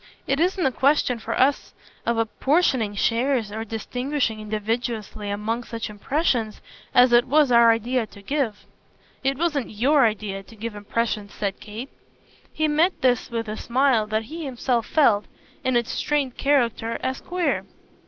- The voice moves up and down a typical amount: Yes, average, 4.0 semitones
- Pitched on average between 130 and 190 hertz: No, high, 235 Hz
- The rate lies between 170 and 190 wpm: No, average, 155 wpm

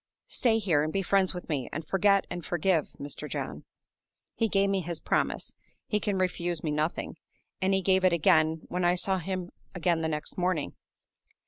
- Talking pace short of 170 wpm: No, average, 190 wpm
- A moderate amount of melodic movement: Yes, average, 3.2 semitones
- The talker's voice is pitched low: No, medium, 180 Hz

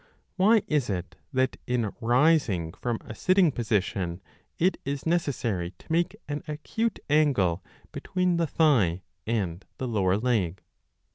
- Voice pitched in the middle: No, low, 125 Hz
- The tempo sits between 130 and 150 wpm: Yes, slow, 135 wpm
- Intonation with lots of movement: Yes, wide, 8.4 semitones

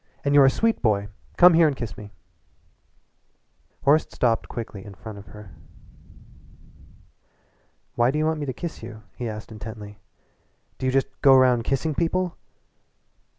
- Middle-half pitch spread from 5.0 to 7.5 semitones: Yes, wide, 5.5 semitones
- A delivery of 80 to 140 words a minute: No, average, 155 wpm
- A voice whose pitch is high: No, low, 125 Hz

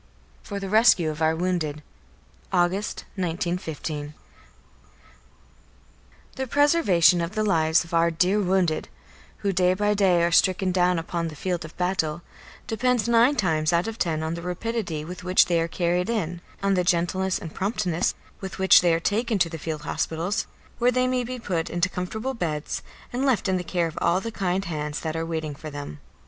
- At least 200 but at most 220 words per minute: No, average, 185 wpm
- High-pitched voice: No, medium, 180 Hz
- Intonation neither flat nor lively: Yes, average, 3.5 semitones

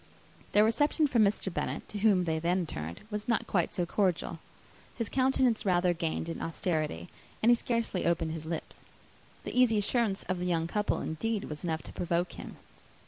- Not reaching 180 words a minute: No, average, 185 wpm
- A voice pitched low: No, medium, 185 Hz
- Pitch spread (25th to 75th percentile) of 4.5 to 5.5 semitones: Yes, average, 5.1 semitones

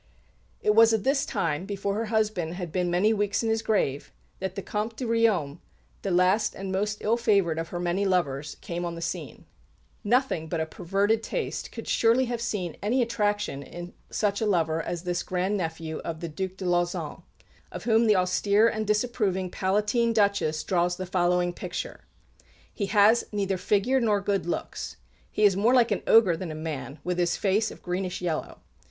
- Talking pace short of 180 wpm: No, average, 190 wpm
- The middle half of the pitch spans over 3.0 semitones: Yes, average, 3.6 semitones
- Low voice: No, high, 195 Hz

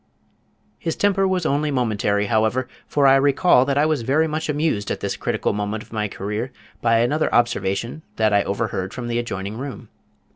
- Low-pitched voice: Yes, low, 120 Hz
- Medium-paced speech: Yes, average, 185 wpm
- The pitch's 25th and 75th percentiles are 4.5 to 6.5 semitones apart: Yes, wide, 5.5 semitones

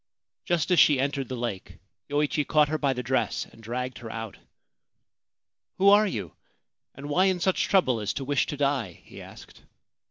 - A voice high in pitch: No, medium, 140 Hz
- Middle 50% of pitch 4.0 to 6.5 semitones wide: Yes, average, 4.4 semitones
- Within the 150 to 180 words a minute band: No, average, 195 wpm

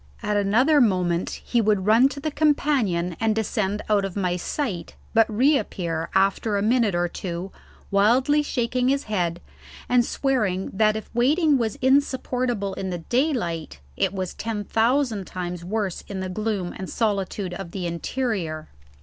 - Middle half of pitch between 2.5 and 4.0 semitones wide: No, average, 5.0 semitones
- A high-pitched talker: Yes, high, 210 Hz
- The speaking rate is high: No, average, 160 wpm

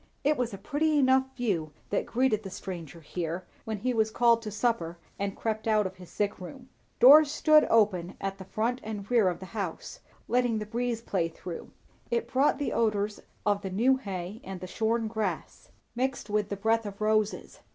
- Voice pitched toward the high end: Yes, high, 215 Hz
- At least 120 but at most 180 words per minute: No, average, 195 wpm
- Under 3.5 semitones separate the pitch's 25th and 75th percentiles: No, average, 4.0 semitones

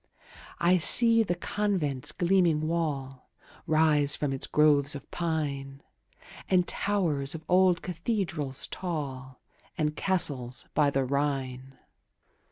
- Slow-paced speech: Yes, slow, 110 wpm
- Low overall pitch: No, medium, 150 Hz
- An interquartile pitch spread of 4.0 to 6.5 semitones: Yes, average, 4.3 semitones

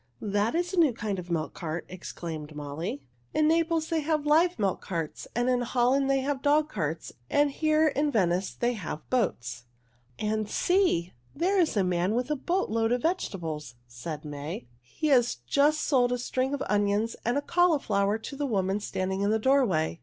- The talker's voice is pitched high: Yes, high, 230 Hz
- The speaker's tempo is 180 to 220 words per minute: Yes, average, 190 wpm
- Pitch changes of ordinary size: No, wide, 8.5 semitones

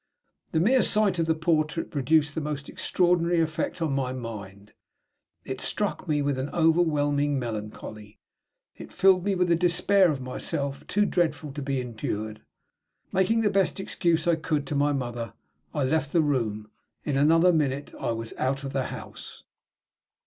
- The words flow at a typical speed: Yes, average, 165 wpm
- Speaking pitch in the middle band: Yes, medium, 150 Hz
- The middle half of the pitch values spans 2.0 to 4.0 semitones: No, average, 4.5 semitones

